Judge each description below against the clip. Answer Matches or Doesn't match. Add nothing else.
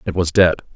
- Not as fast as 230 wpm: Doesn't match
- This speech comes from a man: Matches